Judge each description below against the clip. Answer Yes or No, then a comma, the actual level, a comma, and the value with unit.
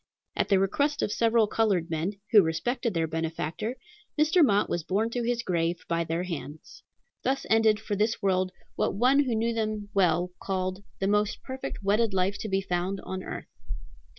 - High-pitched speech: Yes, high, 200 Hz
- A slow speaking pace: No, average, 180 wpm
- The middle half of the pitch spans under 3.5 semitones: No, average, 4.0 semitones